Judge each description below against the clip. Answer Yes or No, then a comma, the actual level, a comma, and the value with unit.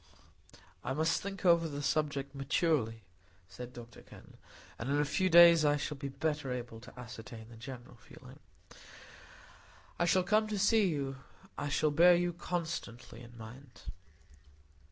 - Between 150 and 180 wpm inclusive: Yes, average, 155 wpm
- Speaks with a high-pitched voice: No, medium, 145 Hz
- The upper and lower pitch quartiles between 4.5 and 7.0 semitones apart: Yes, wide, 5.6 semitones